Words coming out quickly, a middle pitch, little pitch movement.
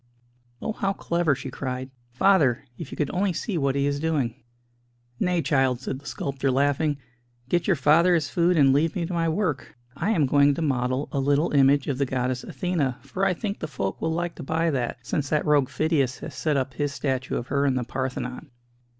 No: fast, 215 wpm; medium, 145 Hz; average, 3.8 semitones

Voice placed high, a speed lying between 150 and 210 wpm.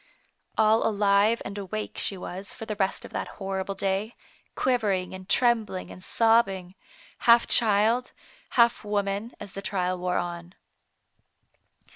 No: high, 200 Hz; average, 140 wpm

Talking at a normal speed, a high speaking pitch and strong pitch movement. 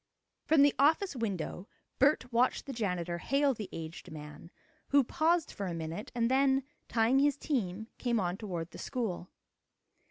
Yes: average, 160 wpm; high, 230 Hz; wide, 7.5 semitones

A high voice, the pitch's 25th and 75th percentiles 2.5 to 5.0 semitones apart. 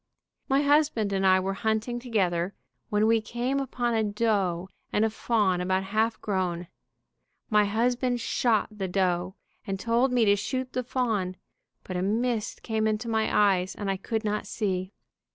Yes: high, 215 Hz; average, 3.6 semitones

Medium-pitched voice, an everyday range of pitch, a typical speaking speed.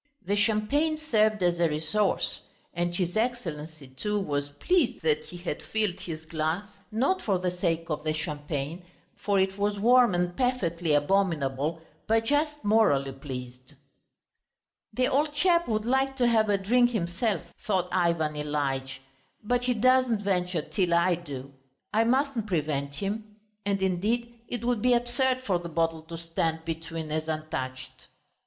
No: medium, 180 Hz; wide, 6.2 semitones; average, 155 wpm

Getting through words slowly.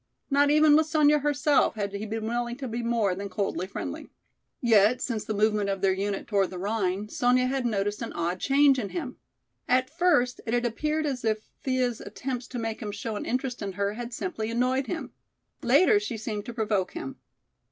No: fast, 205 wpm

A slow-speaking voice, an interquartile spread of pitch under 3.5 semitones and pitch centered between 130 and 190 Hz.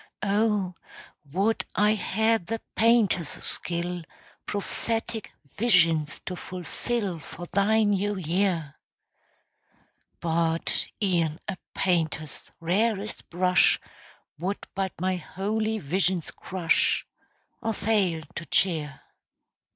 No: slow, 95 wpm; average, 3.8 semitones; medium, 185 Hz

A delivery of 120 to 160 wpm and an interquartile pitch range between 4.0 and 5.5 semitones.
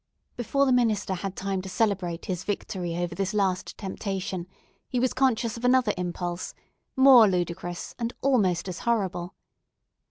Yes: average, 150 wpm; average, 4.5 semitones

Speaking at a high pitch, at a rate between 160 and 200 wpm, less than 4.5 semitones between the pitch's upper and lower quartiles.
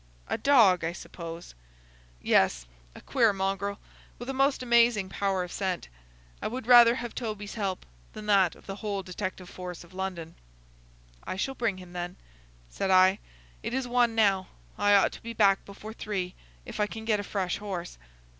Yes: high, 200 Hz; average, 175 wpm; average, 3.6 semitones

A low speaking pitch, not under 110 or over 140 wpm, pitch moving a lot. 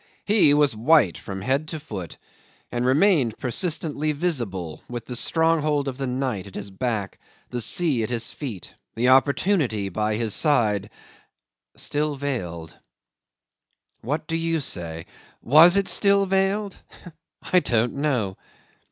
Yes: low, 130 Hz; slow, 135 wpm; wide, 6.4 semitones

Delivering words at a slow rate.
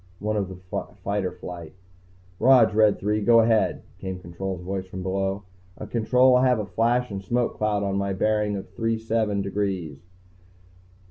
No: average, 170 wpm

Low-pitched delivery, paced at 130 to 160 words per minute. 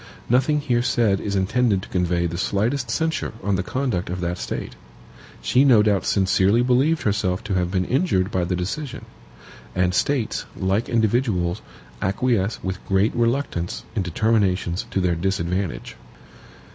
Yes: low, 100 Hz; average, 150 wpm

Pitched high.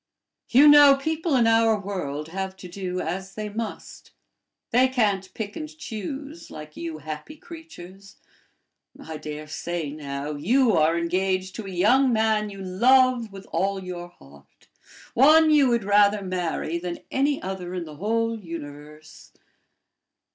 Yes: high, 195 Hz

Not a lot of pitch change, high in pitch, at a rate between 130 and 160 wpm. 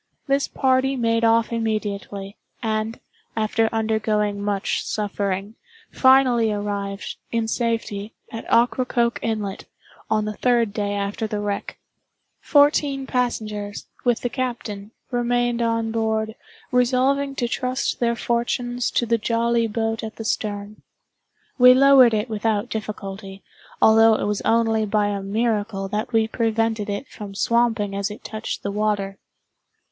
Yes: narrow, 2.3 semitones; high, 225 Hz; slow, 135 wpm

